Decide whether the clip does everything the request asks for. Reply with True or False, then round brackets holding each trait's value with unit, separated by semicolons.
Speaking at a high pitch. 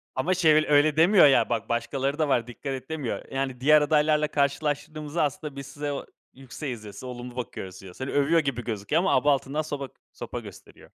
False (140 Hz)